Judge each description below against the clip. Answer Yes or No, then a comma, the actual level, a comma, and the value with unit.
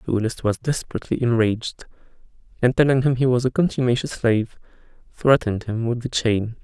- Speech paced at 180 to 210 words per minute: No, average, 165 wpm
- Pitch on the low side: Yes, low, 120 Hz